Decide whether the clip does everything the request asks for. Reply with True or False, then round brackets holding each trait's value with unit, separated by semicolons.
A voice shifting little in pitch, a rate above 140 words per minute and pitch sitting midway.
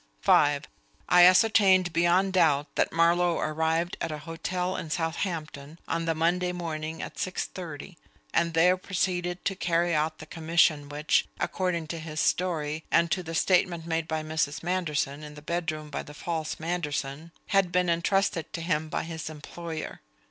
True (2.3 semitones; 165 wpm; 165 Hz)